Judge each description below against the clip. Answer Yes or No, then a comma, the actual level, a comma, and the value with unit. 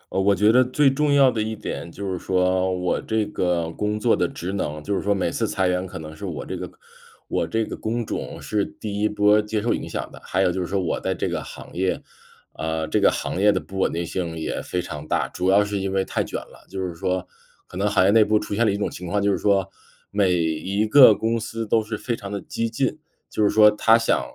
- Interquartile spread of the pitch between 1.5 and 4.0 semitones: Yes, average, 3.0 semitones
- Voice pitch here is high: No, low, 100 Hz